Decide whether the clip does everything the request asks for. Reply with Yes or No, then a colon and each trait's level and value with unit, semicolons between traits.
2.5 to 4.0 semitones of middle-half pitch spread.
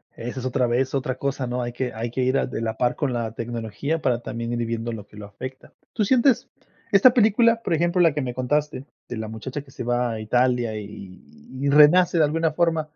No: average, 4.6 semitones